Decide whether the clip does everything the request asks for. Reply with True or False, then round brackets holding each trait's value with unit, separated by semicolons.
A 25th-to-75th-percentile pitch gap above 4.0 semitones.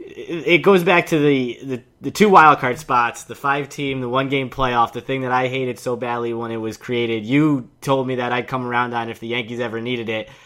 False (2.6 semitones)